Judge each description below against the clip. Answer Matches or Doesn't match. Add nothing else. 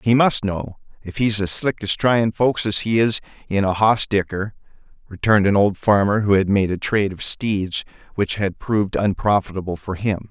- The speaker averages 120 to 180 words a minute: Doesn't match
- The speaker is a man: Matches